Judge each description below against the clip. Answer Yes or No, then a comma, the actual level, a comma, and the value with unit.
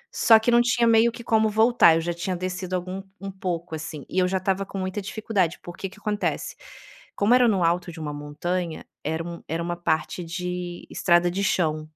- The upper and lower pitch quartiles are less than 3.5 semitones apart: Yes, average, 3.0 semitones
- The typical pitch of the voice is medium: Yes, medium, 180 Hz